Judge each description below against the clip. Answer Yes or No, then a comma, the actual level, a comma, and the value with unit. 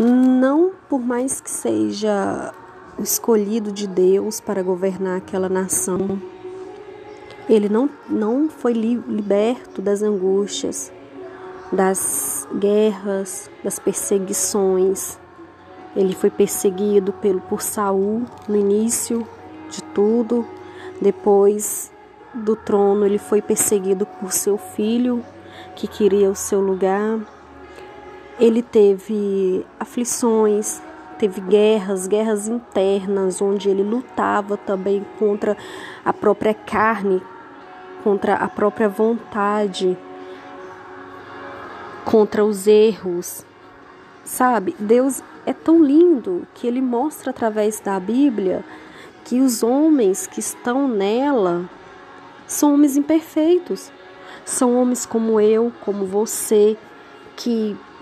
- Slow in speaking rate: Yes, slow, 100 wpm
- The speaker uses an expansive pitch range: No, average, 3.7 semitones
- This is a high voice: Yes, high, 210 Hz